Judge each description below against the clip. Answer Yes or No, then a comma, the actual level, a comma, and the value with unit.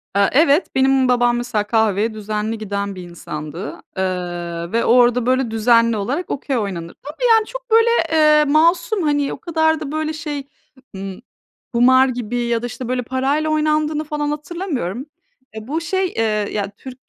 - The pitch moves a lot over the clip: Yes, wide, 5.7 semitones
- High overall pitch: Yes, very high, 255 Hz